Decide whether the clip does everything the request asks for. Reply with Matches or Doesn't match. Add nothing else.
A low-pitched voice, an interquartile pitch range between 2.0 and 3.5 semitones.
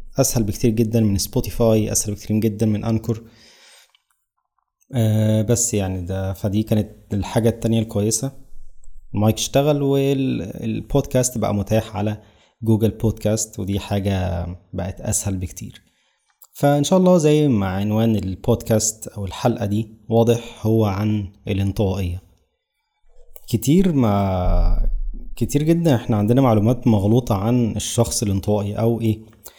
Matches